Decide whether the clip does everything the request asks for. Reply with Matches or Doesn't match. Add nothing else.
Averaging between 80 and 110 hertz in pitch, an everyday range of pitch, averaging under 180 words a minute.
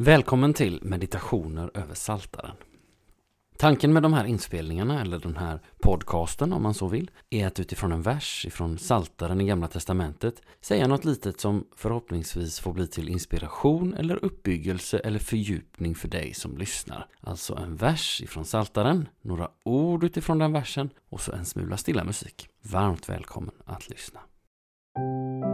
Doesn't match